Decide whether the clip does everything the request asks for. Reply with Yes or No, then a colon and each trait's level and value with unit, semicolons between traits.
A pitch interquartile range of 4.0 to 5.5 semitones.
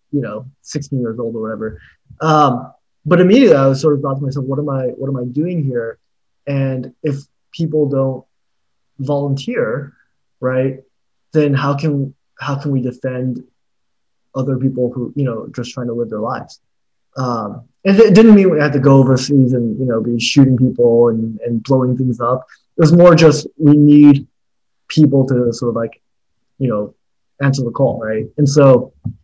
No: average, 3.0 semitones